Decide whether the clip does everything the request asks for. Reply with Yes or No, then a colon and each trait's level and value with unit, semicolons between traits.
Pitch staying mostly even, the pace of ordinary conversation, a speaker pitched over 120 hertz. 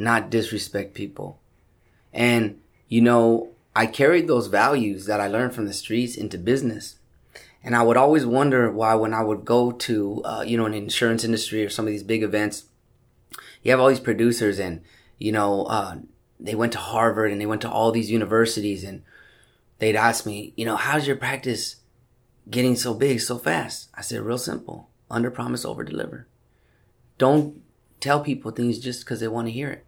No: narrow, 2.2 semitones; average, 190 wpm; low, 115 Hz